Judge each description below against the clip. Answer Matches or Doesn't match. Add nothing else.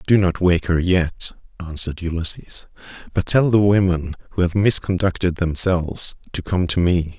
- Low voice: Matches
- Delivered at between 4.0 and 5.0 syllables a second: Matches